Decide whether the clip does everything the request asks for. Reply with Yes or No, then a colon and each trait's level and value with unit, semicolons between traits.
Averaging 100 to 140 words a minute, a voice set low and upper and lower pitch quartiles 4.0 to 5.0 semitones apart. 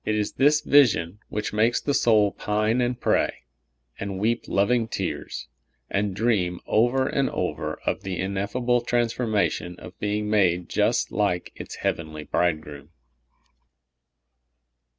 Yes: slow, 135 wpm; low, 105 Hz; average, 4.4 semitones